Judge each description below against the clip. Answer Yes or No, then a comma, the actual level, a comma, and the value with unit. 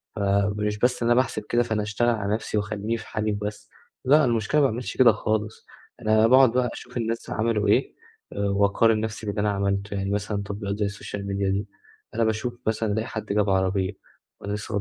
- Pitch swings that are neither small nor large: No, narrow, 2.2 semitones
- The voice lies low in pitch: Yes, low, 105 Hz